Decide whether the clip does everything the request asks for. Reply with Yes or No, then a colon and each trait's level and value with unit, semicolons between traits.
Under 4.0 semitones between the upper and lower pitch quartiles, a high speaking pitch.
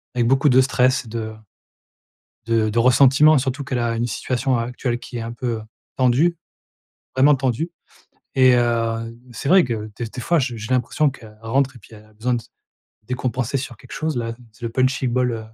No: narrow, 2.4 semitones; low, 125 Hz